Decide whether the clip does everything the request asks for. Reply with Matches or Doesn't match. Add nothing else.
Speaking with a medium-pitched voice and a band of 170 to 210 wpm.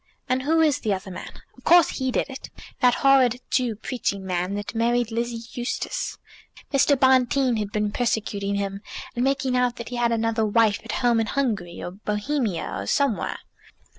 Doesn't match